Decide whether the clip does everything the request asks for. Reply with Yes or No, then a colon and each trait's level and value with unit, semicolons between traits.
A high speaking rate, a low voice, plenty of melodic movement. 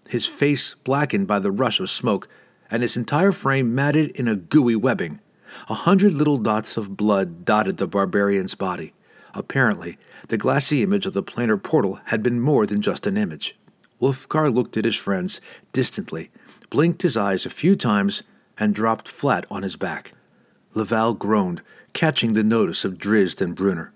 No: average, 175 wpm; low, 115 Hz; wide, 6.3 semitones